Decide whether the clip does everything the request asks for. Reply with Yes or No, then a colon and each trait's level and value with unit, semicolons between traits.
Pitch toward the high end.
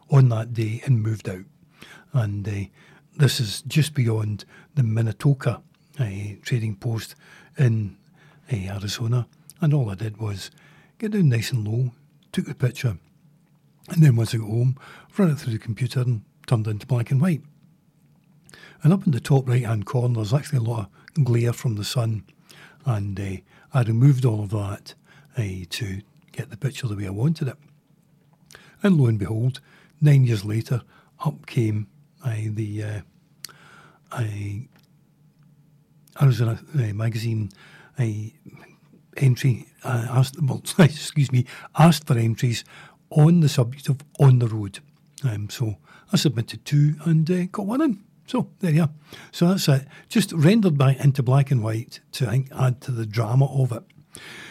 No: low, 135 Hz